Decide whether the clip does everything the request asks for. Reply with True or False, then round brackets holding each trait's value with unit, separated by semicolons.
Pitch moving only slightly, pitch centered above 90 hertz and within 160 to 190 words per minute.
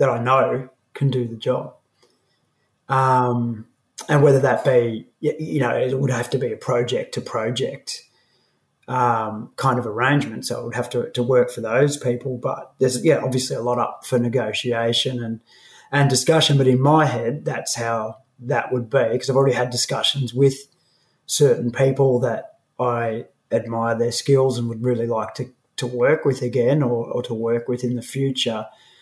True (2.1 semitones; 125 Hz; 180 wpm)